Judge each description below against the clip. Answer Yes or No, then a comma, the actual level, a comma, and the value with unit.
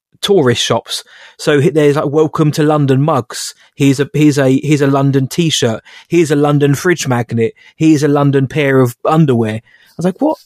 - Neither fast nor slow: Yes, average, 185 wpm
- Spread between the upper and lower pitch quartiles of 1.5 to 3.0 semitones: Yes, narrow, 2.4 semitones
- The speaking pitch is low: No, medium, 145 Hz